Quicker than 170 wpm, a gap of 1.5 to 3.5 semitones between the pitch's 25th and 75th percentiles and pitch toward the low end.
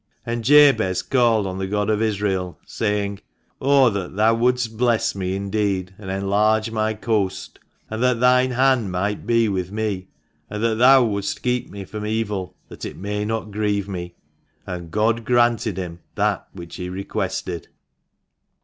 No: average, 165 wpm; average, 3.1 semitones; low, 105 Hz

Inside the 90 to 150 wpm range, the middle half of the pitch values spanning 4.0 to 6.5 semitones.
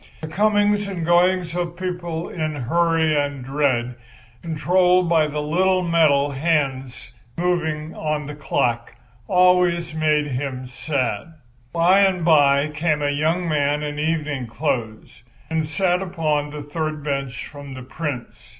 No: average, 140 wpm; average, 3.2 semitones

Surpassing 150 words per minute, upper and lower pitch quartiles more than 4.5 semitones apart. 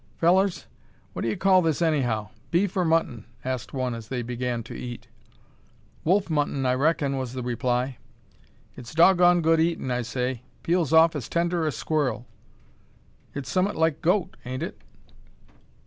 Yes: average, 160 wpm; average, 5.2 semitones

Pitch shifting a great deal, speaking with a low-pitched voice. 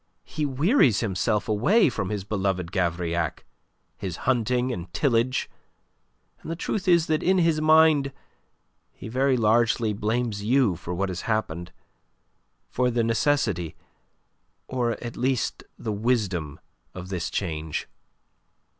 Yes: wide, 5.9 semitones; low, 115 Hz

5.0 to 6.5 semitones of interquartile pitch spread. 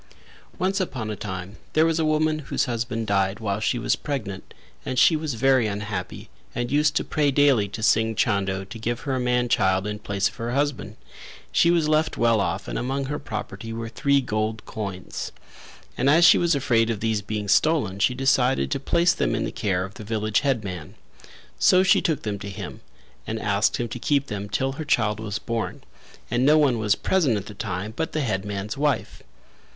Yes: average, 5.3 semitones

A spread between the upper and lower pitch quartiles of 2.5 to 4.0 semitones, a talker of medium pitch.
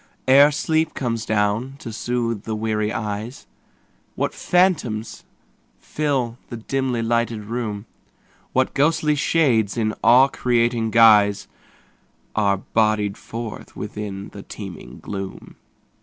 No: average, 3.5 semitones; low, 115 Hz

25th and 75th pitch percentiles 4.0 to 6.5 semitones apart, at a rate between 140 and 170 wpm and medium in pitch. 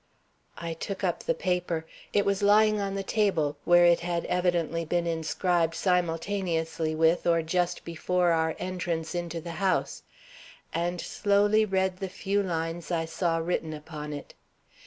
No: narrow, 2.5 semitones; average, 155 wpm; medium, 175 Hz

